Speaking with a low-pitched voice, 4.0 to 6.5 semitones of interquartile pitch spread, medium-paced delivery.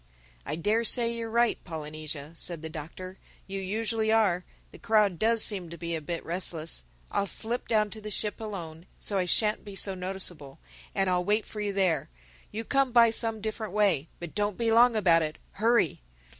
No: high, 200 Hz; average, 4.6 semitones; average, 185 wpm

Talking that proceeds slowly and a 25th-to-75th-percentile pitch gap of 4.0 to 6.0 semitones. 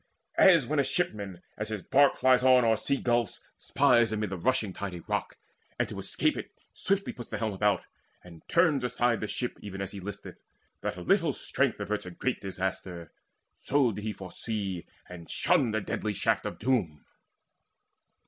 No: average, 185 wpm; average, 4.9 semitones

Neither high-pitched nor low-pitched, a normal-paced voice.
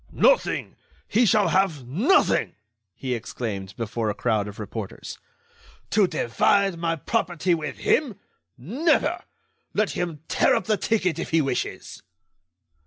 No: medium, 165 Hz; slow, 130 wpm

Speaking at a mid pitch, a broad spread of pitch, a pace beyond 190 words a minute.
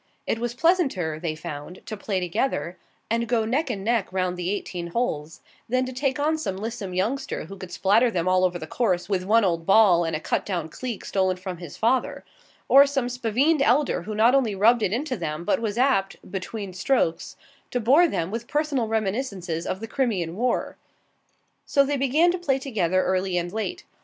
No: high, 215 Hz; wide, 5.8 semitones; average, 200 wpm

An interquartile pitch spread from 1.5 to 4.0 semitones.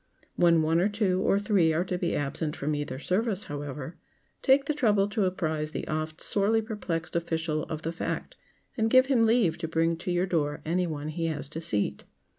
No: average, 4.5 semitones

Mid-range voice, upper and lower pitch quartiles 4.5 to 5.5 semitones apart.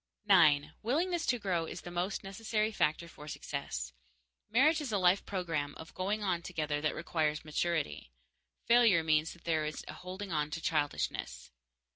Yes: medium, 175 Hz; average, 5.0 semitones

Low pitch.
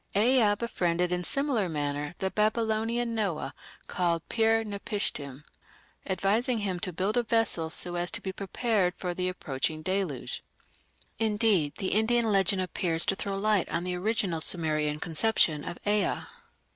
No: high, 190 Hz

